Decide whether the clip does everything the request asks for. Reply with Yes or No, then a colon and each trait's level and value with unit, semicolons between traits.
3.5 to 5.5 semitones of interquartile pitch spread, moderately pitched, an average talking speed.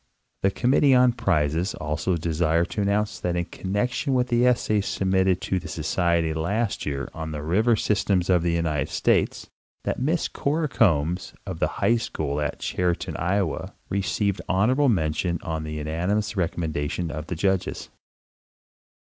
No: average, 4.6 semitones; very low, 90 Hz; average, 160 wpm